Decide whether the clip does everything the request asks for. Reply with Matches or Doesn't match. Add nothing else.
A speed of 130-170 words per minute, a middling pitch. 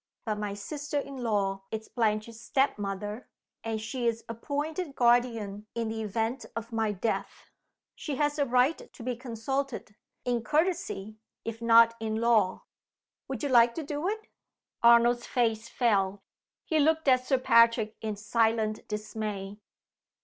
Doesn't match